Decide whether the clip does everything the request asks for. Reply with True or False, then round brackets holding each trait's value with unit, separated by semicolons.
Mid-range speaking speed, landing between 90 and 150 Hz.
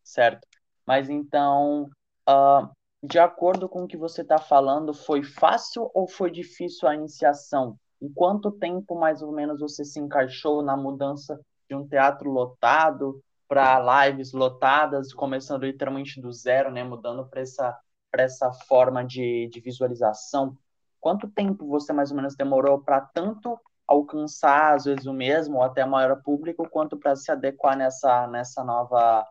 True (160 wpm; 140 Hz)